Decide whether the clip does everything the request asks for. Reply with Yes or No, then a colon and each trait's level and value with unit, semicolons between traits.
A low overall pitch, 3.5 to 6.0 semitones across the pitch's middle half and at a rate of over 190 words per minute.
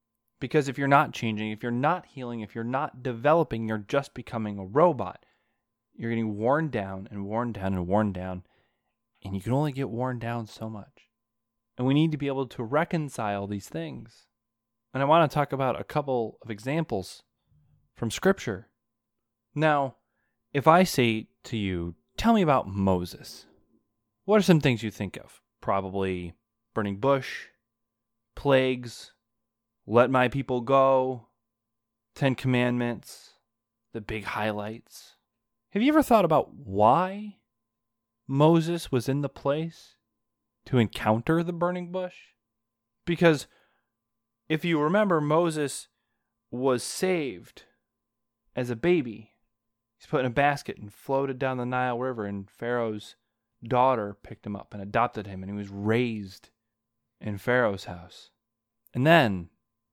No: low, 115 Hz; average, 3.8 semitones; average, 145 wpm